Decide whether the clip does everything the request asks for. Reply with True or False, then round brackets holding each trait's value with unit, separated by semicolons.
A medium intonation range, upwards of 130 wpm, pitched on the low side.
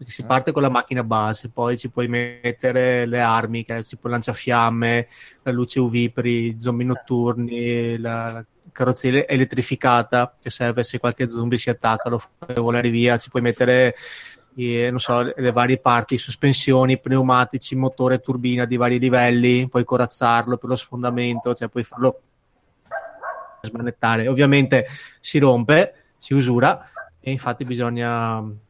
False (1.2 semitones; 145 wpm; 125 Hz)